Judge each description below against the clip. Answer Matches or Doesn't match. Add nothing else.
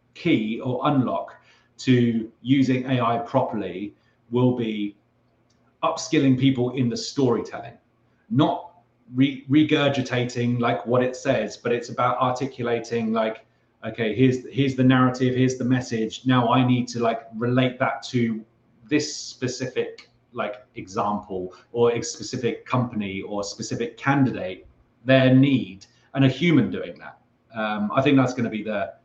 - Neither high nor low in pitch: Doesn't match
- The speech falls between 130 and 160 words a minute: Matches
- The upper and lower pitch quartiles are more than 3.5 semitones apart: Doesn't match